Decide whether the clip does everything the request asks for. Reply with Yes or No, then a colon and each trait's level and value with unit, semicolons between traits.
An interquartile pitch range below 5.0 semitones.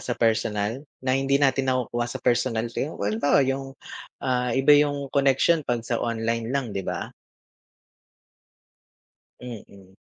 Yes: average, 3.0 semitones